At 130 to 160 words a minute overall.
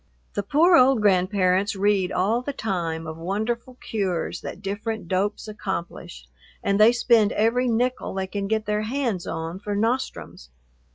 Yes: average, 155 wpm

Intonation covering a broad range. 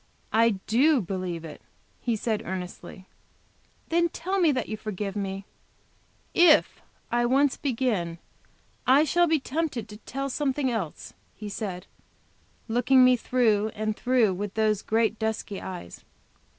No: average, 4.7 semitones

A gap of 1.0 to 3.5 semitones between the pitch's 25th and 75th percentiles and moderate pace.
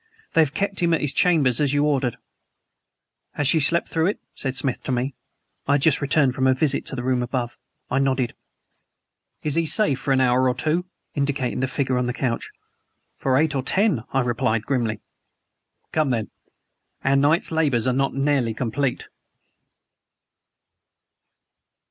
Yes: average, 2.9 semitones; average, 170 wpm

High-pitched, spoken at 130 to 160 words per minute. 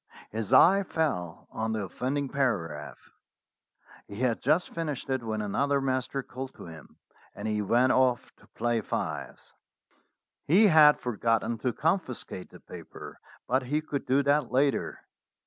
No: low, 130 Hz; average, 150 wpm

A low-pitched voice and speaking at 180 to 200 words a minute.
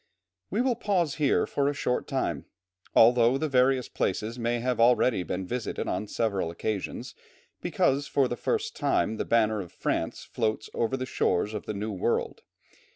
No: low, 120 Hz; average, 170 wpm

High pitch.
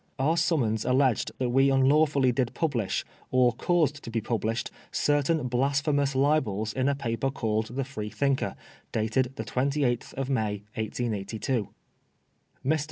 No: low, 130 Hz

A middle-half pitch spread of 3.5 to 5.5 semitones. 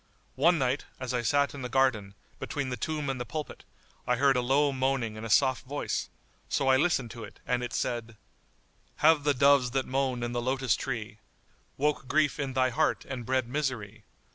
No: narrow, 2.6 semitones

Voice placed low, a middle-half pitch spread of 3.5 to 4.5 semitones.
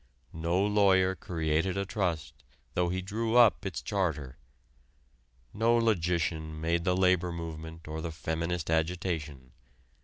No: very low, 85 Hz; average, 2.9 semitones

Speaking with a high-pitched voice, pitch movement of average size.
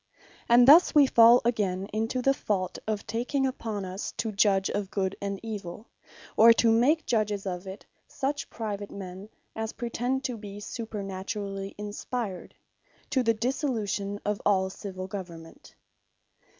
Yes: high, 210 Hz; average, 3.2 semitones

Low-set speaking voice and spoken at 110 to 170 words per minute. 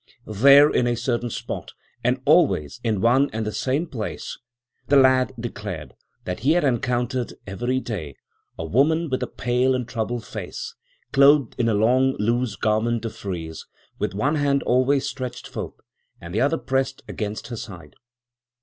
Yes: low, 120 Hz; average, 165 wpm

